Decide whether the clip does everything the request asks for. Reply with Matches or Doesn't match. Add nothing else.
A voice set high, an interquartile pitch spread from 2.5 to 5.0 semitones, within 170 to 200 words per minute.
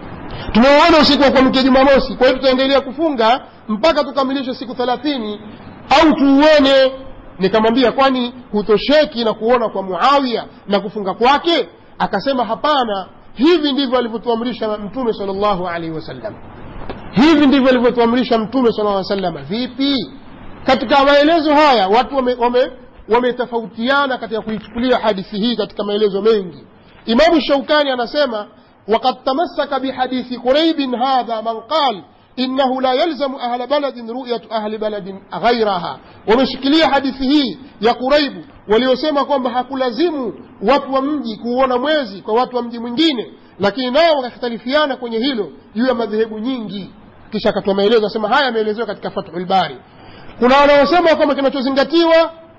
Doesn't match